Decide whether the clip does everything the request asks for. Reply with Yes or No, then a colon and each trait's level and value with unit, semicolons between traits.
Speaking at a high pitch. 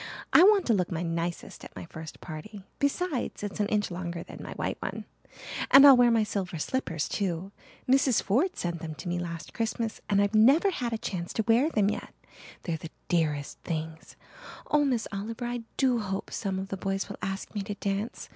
Yes: high, 200 Hz